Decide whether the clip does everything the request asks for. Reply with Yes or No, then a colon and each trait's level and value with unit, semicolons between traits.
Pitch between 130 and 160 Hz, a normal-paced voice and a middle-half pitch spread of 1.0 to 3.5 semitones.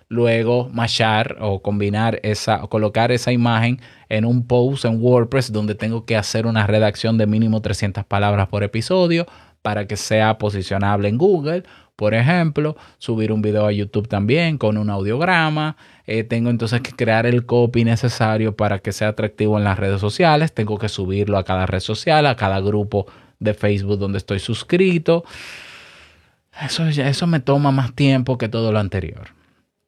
No: low, 110 Hz; average, 170 wpm; average, 3.0 semitones